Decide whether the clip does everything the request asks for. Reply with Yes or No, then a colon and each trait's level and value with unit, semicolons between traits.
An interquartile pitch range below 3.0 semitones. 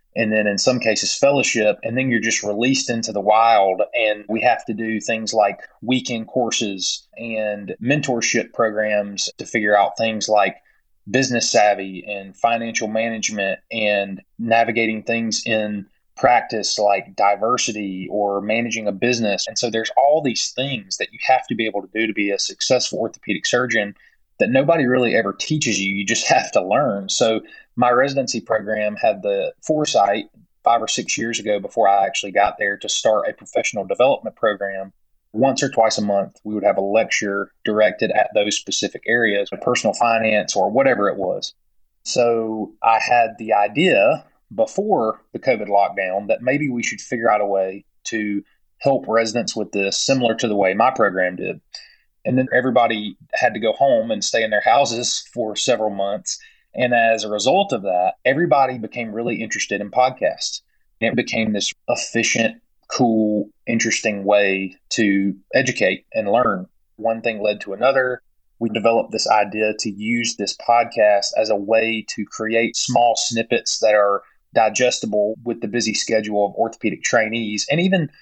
Yes: narrow, 2.4 semitones